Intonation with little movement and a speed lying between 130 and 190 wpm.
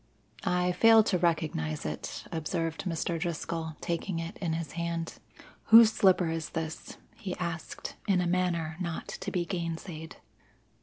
Yes: narrow, 1.9 semitones; average, 145 wpm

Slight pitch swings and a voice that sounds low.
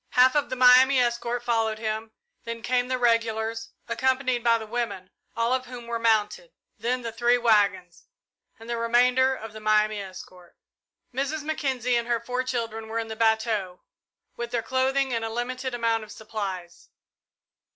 No: narrow, 2.2 semitones; high, 235 Hz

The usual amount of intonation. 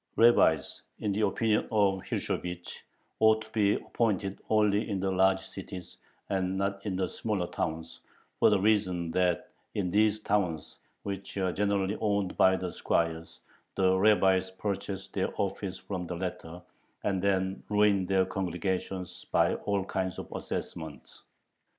No: narrow, 1.9 semitones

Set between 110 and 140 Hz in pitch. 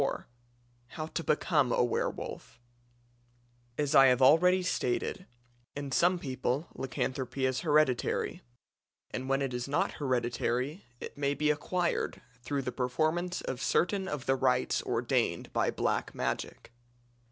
Yes: low, 135 Hz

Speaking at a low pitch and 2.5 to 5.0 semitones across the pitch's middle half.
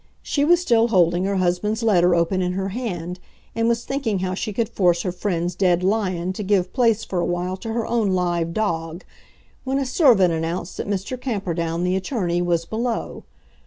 No: medium, 185 Hz; average, 4.2 semitones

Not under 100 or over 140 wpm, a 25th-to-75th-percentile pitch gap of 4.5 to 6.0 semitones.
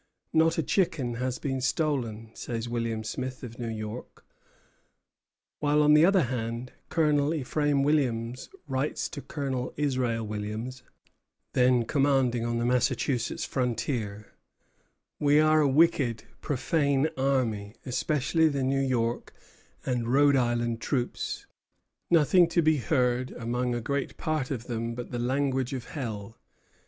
No: slow, 135 wpm; average, 3.5 semitones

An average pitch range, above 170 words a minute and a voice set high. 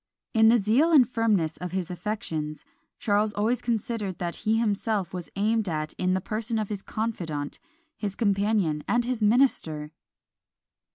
No: average, 3.9 semitones; average, 155 wpm; high, 210 Hz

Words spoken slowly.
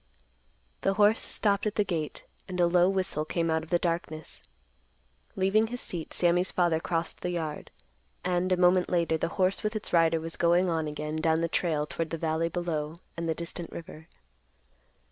No: average, 185 wpm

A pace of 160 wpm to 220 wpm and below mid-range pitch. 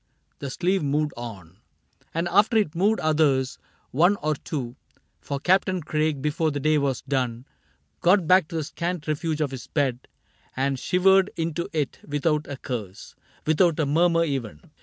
No: average, 170 wpm; medium, 150 Hz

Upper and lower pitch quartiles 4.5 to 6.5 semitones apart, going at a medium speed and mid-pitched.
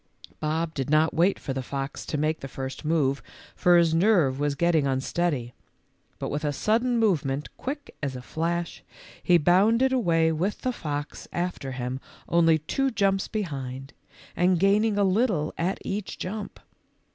Yes: wide, 5.4 semitones; average, 160 wpm; medium, 165 Hz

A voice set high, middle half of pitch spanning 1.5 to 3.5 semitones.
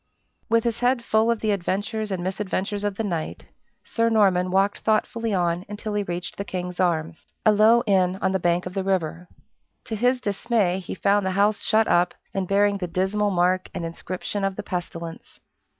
Yes: high, 195 Hz; average, 2.9 semitones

